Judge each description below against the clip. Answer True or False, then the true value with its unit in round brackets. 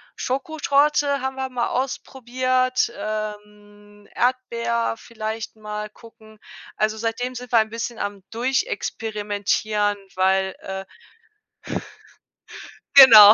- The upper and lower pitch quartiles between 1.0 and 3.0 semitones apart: False (3.4 semitones)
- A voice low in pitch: False (225 Hz)